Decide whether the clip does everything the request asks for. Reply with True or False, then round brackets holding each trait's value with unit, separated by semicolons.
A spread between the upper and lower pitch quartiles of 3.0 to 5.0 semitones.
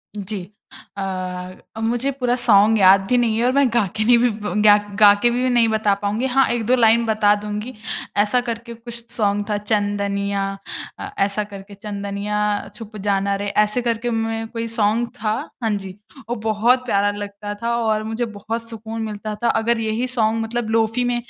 False (2.4 semitones)